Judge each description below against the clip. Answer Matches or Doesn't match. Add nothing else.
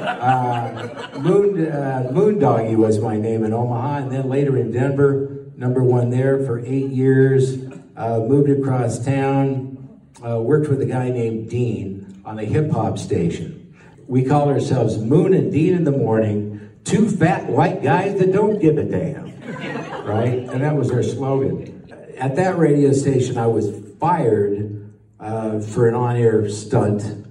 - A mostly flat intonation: Doesn't match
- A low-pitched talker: Matches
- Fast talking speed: Doesn't match